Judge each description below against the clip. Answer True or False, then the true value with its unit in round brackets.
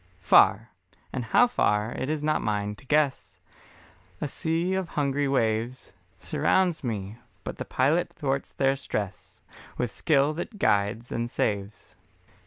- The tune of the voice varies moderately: False (5.8 semitones)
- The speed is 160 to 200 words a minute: False (140 wpm)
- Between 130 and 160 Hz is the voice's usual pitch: True (135 Hz)